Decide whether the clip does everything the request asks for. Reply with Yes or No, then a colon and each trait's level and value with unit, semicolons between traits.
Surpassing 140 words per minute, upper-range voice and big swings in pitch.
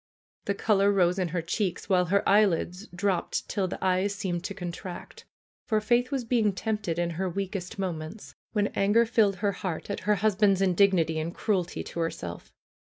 No: average, 180 wpm; high, 195 Hz; average, 2.7 semitones